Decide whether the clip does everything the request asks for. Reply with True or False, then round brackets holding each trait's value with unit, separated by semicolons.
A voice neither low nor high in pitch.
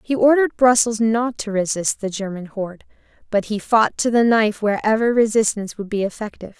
False (220 Hz)